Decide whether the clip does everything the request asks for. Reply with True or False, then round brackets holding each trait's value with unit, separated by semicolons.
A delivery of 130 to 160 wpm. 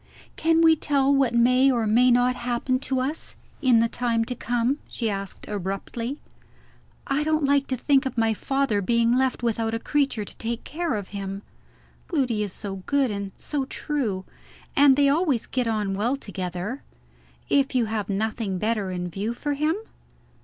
False (175 wpm)